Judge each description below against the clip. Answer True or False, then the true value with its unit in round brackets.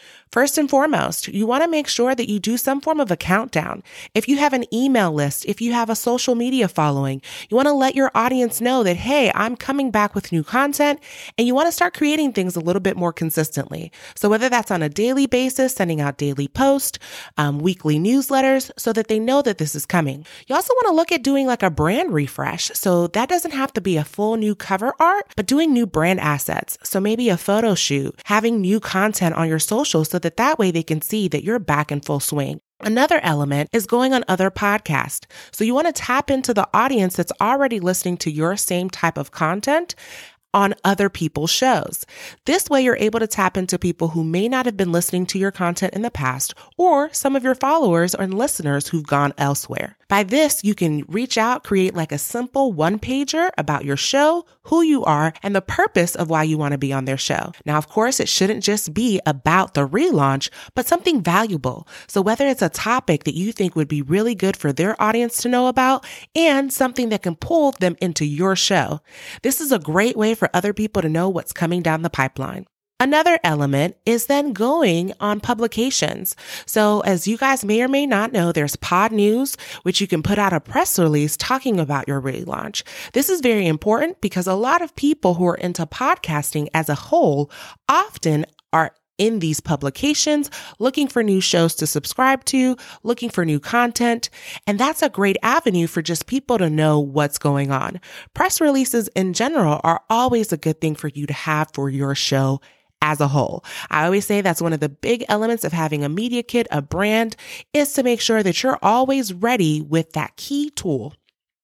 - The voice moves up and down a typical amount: False (7.6 semitones)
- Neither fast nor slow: False (215 wpm)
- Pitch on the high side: True (205 Hz)